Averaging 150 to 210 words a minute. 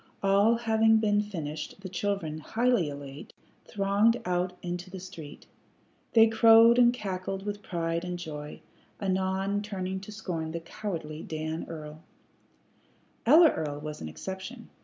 No: average, 140 wpm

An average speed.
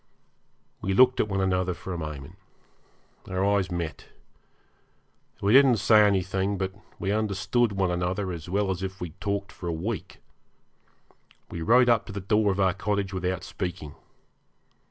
Yes: average, 165 wpm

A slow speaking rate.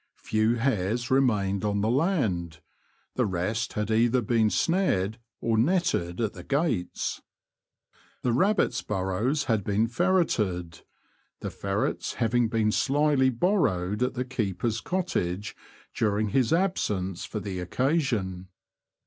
Yes: slow, 125 wpm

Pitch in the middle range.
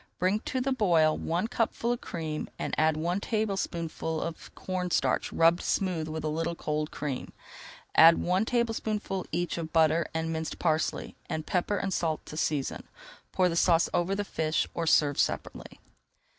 Yes: medium, 170 Hz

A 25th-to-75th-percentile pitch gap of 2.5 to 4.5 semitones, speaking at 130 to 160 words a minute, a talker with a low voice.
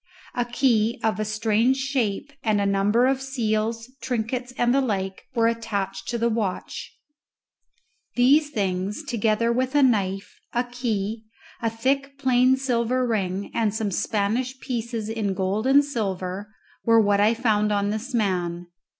No: average, 3.4 semitones; average, 150 wpm; high, 225 Hz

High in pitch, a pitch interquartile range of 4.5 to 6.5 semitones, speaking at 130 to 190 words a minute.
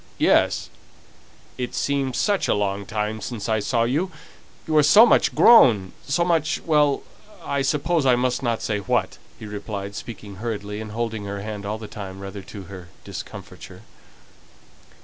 No: low, 110 Hz; wide, 5.5 semitones; average, 160 wpm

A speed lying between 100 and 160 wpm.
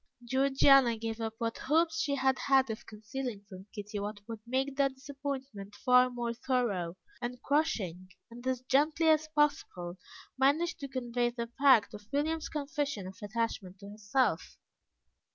Yes: average, 150 wpm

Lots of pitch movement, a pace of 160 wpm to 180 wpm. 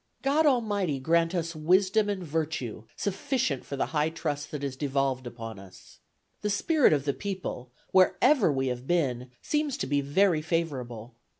Yes: wide, 6.5 semitones; average, 165 wpm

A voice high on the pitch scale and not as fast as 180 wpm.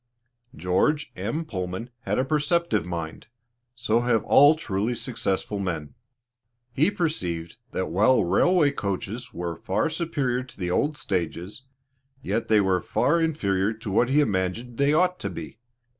No: low, 115 Hz; average, 150 wpm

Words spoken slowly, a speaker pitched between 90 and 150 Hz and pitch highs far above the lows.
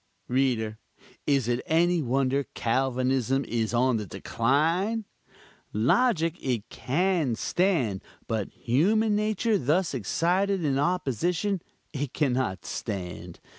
Yes: slow, 110 wpm; low, 135 Hz; wide, 6.8 semitones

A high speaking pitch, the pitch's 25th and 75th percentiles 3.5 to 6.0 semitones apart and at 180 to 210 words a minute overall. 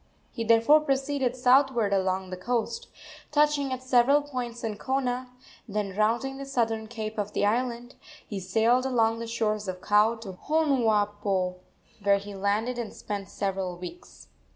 No: high, 230 Hz; average, 3.9 semitones; average, 150 wpm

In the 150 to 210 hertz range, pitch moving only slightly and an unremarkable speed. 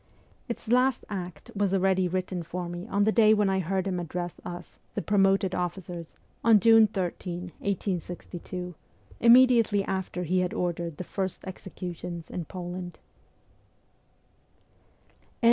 No: medium, 185 Hz; narrow, 2.1 semitones; slow, 130 wpm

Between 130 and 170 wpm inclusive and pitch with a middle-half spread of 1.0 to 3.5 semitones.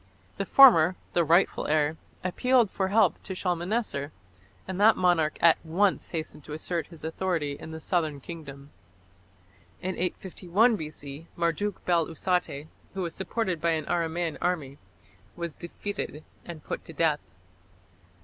Yes: average, 140 wpm; average, 3.0 semitones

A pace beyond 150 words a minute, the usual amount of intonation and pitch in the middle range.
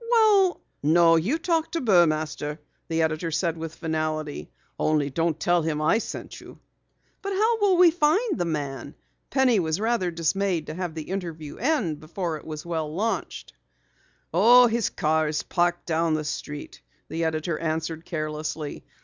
No: average, 165 wpm; wide, 6.3 semitones; medium, 165 Hz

